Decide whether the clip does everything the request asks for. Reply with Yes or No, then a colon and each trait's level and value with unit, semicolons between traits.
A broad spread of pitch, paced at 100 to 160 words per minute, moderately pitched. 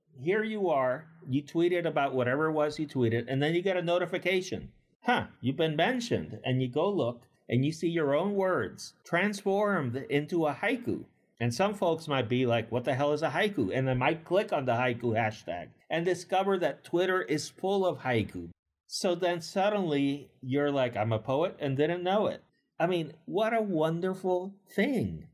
No: wide, 5.9 semitones; average, 190 wpm; medium, 155 Hz